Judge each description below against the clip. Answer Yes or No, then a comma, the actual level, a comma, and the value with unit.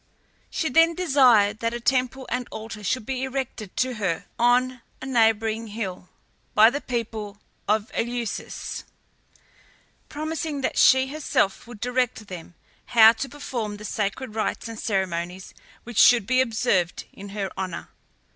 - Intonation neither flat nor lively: Yes, average, 3.7 semitones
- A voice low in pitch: No, high, 230 Hz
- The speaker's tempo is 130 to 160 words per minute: Yes, average, 145 wpm